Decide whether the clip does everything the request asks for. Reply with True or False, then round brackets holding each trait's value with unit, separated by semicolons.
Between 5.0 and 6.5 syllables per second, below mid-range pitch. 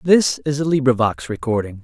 True (5.3 syllables/s; 130 Hz)